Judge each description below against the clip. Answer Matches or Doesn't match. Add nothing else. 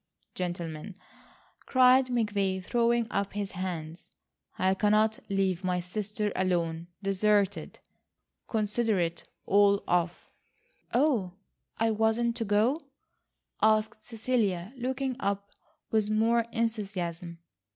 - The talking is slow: Matches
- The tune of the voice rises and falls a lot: Doesn't match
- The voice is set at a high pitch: Matches